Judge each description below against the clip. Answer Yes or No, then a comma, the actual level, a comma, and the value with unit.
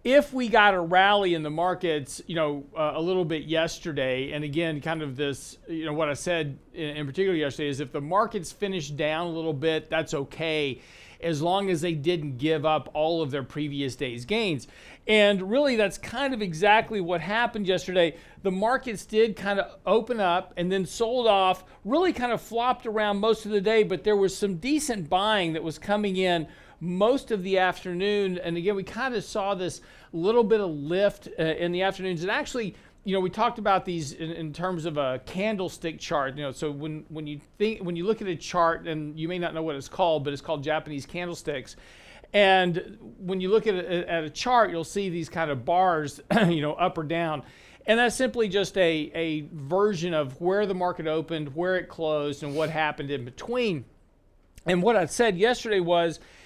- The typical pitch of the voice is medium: Yes, medium, 175 Hz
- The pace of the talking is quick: Yes, fast, 210 wpm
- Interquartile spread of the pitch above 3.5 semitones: Yes, average, 4.7 semitones